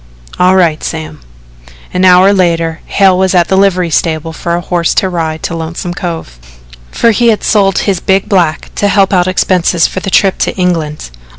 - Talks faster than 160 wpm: Yes, average, 190 wpm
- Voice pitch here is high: No, medium, 180 Hz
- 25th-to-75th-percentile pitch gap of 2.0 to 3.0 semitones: Yes, narrow, 2.4 semitones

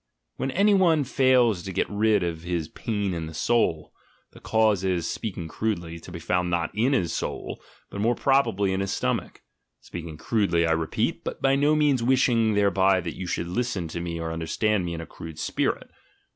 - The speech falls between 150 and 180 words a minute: No, average, 200 wpm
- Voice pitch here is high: No, very low, 95 Hz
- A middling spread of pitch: No, wide, 5.7 semitones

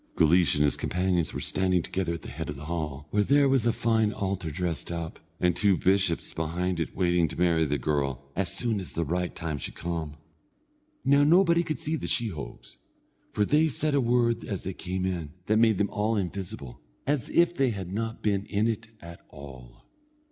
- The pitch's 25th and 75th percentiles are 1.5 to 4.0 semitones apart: No, wide, 5.6 semitones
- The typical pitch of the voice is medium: No, very low, 95 Hz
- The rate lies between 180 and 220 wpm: Yes, fast, 205 wpm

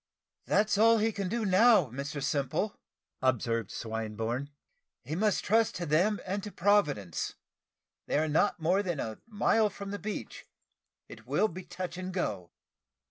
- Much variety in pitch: Yes, wide, 7.0 semitones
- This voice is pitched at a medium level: Yes, medium, 180 Hz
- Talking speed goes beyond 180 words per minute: No, average, 155 wpm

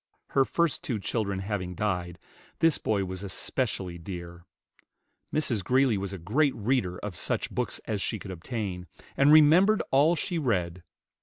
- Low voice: Yes, low, 105 Hz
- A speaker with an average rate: Yes, average, 155 wpm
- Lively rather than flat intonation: Yes, wide, 6.9 semitones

